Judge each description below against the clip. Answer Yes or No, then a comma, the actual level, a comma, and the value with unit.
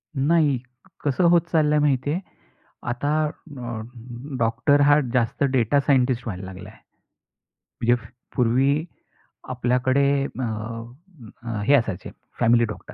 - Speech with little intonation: No, average, 3.8 semitones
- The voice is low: Yes, low, 130 Hz